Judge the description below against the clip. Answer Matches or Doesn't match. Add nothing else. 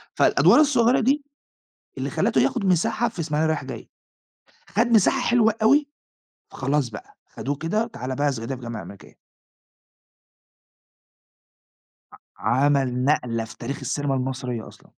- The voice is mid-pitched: Matches